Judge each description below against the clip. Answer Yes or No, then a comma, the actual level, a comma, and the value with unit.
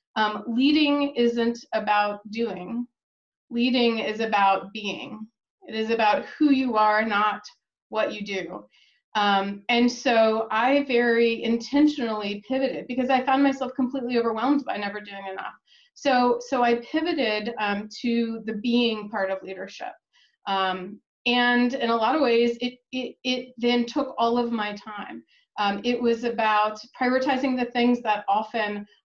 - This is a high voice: Yes, high, 235 Hz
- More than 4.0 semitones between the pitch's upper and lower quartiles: No, average, 3.0 semitones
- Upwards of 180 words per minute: No, average, 150 wpm